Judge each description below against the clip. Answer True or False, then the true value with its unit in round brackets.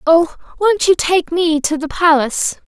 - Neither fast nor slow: True (180 wpm)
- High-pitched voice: True (330 Hz)